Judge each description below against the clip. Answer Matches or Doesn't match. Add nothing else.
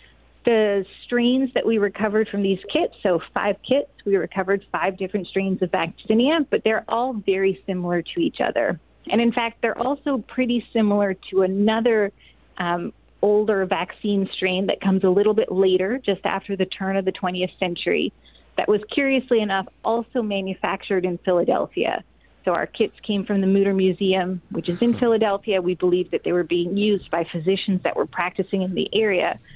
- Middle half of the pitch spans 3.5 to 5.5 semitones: Doesn't match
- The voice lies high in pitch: Matches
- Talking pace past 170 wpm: Matches